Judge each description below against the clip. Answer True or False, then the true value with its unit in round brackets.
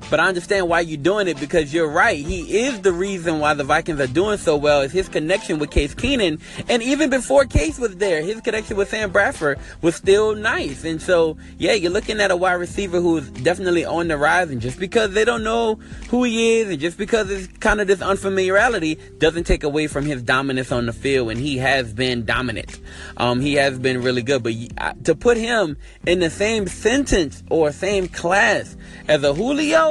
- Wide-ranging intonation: True (6.6 semitones)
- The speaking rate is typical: False (215 wpm)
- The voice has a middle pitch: True (175 Hz)